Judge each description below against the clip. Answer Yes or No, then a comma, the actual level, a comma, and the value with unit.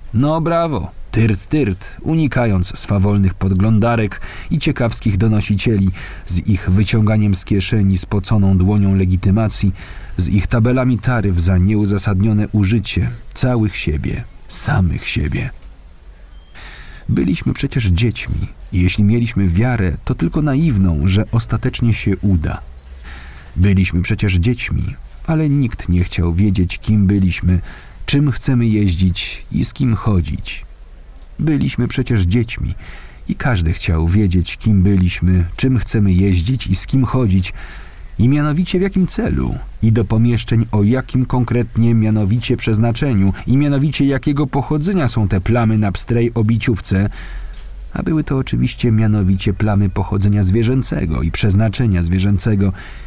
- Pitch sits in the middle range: No, low, 105 Hz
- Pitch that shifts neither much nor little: Yes, average, 4.3 semitones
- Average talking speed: Yes, average, 125 wpm